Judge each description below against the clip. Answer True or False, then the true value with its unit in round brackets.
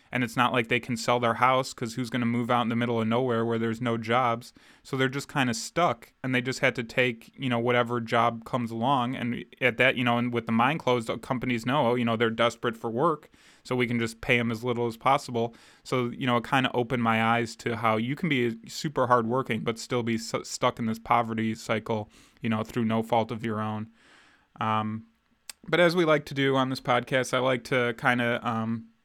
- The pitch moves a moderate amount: False (1.8 semitones)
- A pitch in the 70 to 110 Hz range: False (120 Hz)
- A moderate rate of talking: False (245 wpm)